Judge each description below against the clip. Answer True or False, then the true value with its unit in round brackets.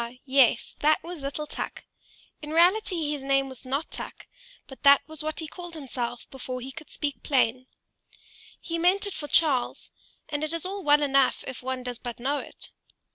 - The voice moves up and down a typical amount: True (3.5 semitones)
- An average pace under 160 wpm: False (185 wpm)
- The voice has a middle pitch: False (290 Hz)